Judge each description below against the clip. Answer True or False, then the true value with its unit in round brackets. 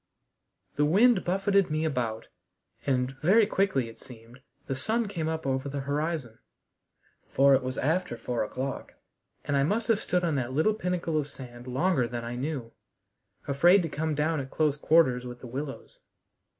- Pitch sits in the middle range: True (145 Hz)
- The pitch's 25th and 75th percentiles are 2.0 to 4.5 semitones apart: False (5.2 semitones)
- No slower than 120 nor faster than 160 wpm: False (175 wpm)